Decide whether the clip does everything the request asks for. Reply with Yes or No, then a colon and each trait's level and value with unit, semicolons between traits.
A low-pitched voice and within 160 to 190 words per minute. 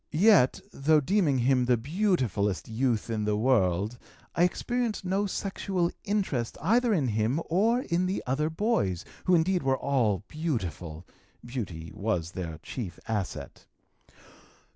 No: low, 130 Hz; slow, 135 wpm